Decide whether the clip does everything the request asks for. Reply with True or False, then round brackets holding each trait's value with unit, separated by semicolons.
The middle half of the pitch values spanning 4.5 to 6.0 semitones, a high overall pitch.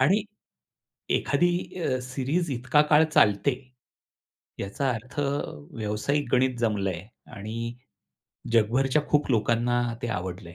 False (4.8 semitones; 120 Hz)